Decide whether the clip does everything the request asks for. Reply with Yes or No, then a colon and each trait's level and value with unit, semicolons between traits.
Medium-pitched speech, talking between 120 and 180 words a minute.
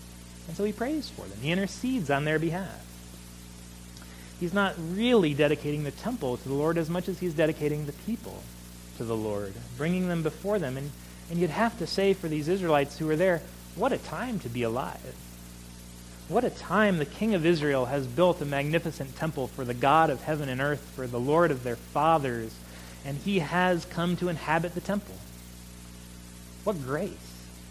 No: medium, 145 Hz; average, 190 wpm